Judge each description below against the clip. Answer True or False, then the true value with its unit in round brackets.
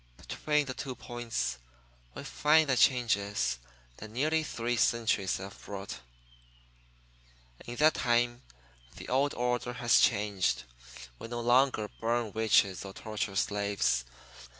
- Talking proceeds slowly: True (125 wpm)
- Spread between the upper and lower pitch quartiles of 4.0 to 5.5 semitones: False (3.5 semitones)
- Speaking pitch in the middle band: False (120 Hz)